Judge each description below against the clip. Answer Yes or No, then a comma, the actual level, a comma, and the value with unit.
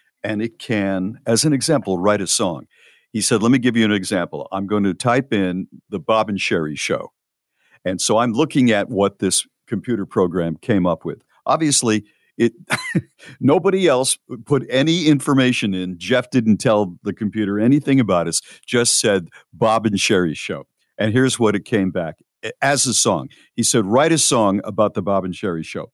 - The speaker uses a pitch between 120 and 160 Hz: No, low, 110 Hz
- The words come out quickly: No, average, 185 wpm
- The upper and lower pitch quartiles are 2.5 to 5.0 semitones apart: Yes, average, 4.5 semitones